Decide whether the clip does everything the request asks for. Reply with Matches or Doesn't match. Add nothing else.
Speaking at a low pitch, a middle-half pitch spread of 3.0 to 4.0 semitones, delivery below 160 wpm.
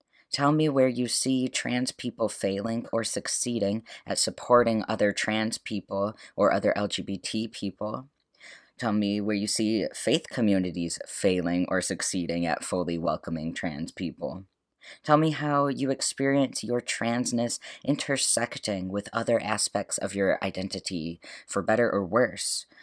Doesn't match